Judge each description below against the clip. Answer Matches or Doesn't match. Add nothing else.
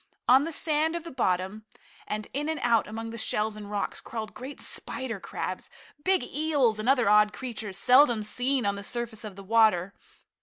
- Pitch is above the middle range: Matches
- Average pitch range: Matches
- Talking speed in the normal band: Matches